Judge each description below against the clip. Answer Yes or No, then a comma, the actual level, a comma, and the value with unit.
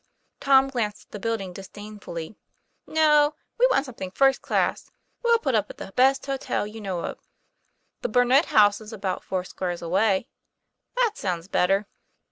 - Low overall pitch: No, high, 215 Hz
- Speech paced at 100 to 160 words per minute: Yes, average, 155 wpm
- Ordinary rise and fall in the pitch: No, wide, 5.9 semitones